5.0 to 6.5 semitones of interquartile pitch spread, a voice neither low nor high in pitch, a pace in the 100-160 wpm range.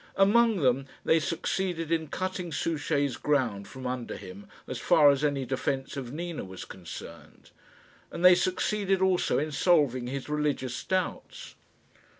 Yes: average, 5.3 semitones; medium, 150 Hz; average, 145 wpm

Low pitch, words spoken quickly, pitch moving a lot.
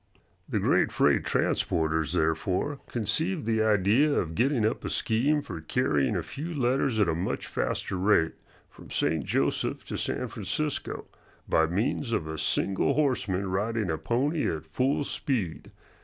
No: low, 105 Hz; average, 155 wpm; wide, 8.2 semitones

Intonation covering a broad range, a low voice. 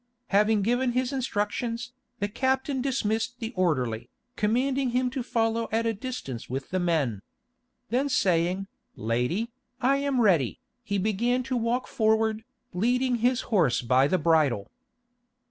No: wide, 5.9 semitones; high, 225 Hz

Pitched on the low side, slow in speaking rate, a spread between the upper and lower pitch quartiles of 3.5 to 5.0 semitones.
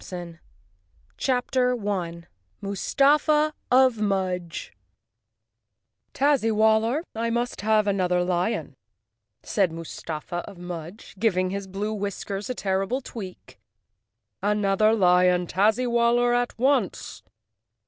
No: high, 205 Hz; slow, 105 wpm; average, 4.7 semitones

